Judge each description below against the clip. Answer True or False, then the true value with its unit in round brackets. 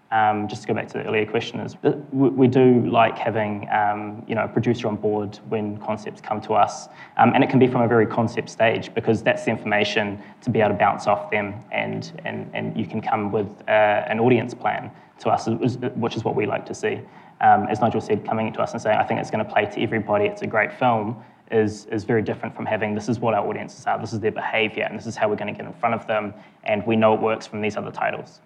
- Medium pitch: False (110 Hz)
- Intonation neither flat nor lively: False (1.8 semitones)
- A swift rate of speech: True (265 wpm)